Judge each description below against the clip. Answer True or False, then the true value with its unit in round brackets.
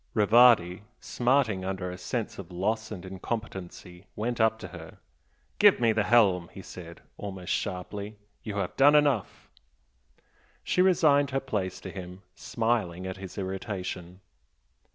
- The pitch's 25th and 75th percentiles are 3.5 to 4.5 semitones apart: True (4.2 semitones)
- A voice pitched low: True (100 Hz)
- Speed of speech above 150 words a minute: False (140 wpm)